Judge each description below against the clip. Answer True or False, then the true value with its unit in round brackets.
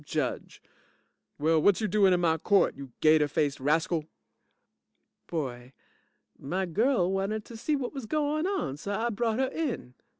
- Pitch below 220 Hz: True (190 Hz)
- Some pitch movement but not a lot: False (7.1 semitones)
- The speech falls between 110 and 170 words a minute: True (160 wpm)